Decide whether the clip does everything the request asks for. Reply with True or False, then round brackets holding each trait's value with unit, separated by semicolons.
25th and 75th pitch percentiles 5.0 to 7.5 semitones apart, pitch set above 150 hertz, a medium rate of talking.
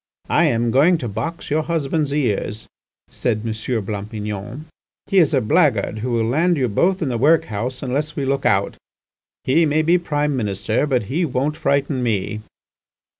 False (5.6 semitones; 130 Hz; 170 wpm)